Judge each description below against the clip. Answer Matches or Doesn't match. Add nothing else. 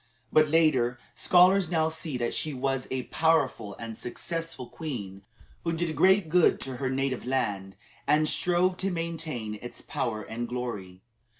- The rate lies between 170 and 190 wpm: Doesn't match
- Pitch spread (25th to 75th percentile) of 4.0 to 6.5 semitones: Matches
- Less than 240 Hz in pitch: Matches